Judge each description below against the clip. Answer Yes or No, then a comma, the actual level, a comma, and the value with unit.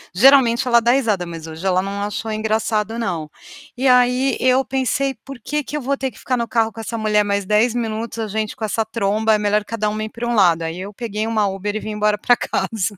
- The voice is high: Yes, high, 220 Hz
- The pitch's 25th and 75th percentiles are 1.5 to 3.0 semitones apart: Yes, average, 2.7 semitones